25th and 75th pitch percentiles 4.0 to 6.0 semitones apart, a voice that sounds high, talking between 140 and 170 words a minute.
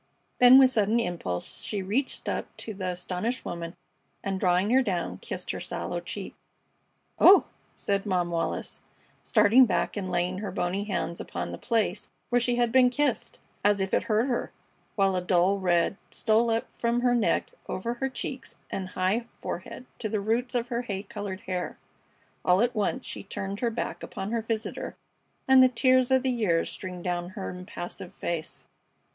No: average, 4.6 semitones; high, 205 Hz; average, 180 wpm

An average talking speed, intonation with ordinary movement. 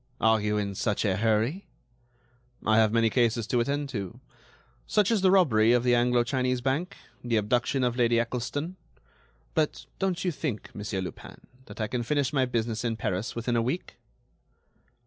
Yes: average, 175 wpm; average, 3.6 semitones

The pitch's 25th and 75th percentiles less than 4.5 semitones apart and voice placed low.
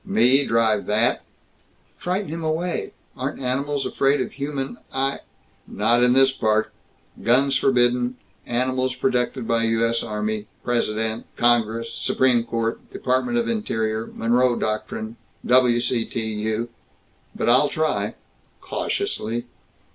Yes: average, 2.9 semitones; low, 120 Hz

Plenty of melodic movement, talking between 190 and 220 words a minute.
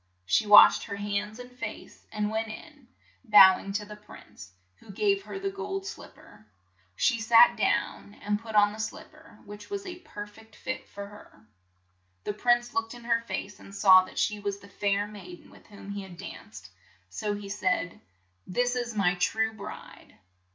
No: average, 2.7 semitones; average, 200 wpm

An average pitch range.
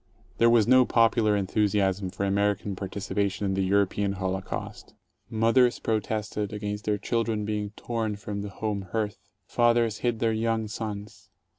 No: narrow, 2.0 semitones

